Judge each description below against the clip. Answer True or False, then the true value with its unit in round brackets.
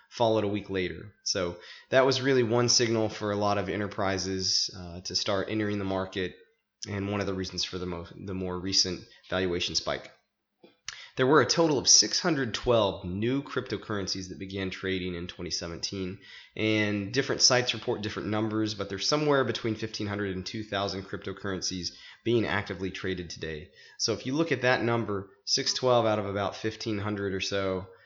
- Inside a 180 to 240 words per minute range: False (170 wpm)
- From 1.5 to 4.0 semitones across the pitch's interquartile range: True (2.7 semitones)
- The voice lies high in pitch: False (100 Hz)